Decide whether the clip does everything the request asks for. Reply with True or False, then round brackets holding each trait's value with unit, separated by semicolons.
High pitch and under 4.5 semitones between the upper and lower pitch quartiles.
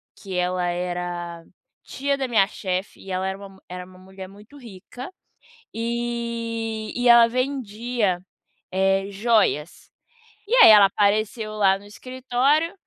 True (210 Hz; 4.0 semitones)